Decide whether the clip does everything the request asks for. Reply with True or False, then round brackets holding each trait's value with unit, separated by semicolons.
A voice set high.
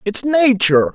True (220 Hz)